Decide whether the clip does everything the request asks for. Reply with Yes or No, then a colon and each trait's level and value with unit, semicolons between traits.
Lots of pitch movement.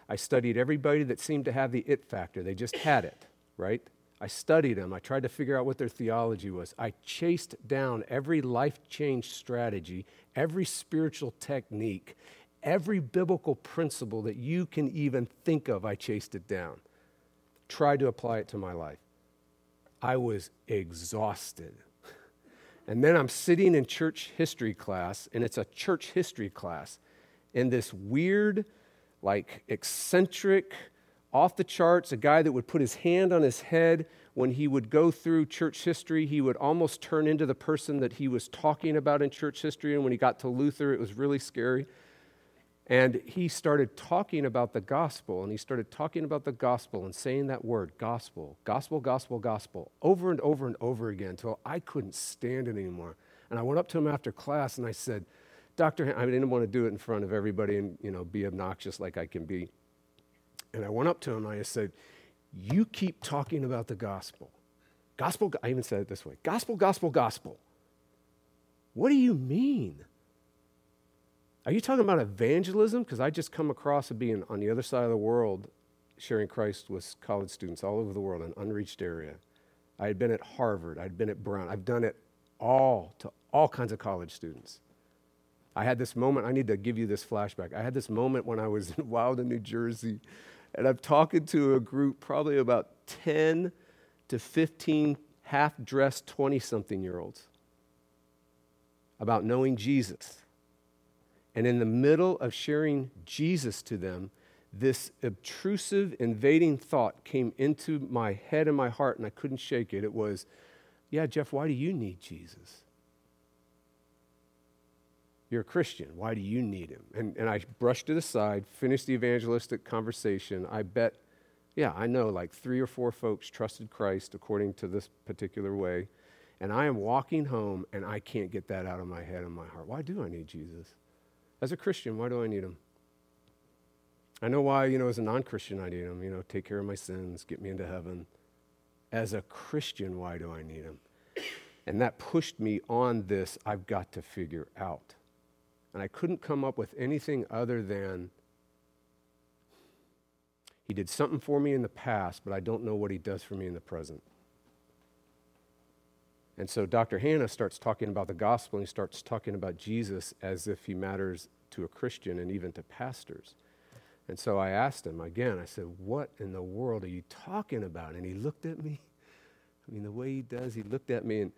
Yes: wide, 7.7 semitones